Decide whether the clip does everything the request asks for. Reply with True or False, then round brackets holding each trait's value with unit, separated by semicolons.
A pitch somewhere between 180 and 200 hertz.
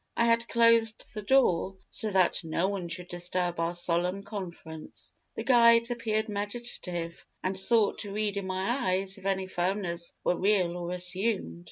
True (190 Hz)